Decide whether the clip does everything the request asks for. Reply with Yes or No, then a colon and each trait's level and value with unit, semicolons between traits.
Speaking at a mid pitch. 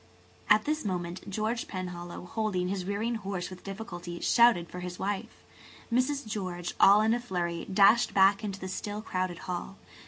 No: high, 195 Hz